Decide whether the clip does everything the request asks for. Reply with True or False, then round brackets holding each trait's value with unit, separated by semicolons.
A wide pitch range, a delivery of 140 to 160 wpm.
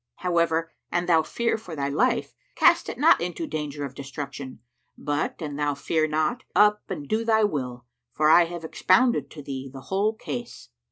False (6.5 semitones; 180 wpm)